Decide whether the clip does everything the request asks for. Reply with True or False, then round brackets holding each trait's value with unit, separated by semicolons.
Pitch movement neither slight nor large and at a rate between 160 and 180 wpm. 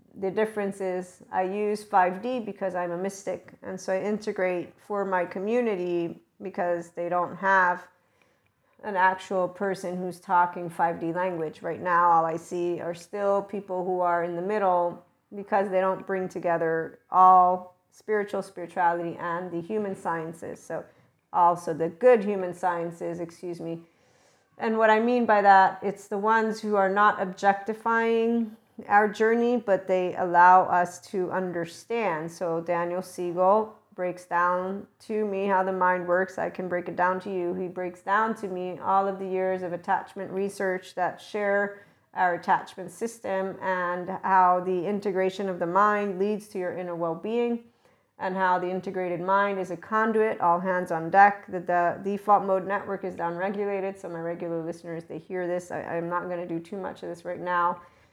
False (2.2 semitones; 175 wpm)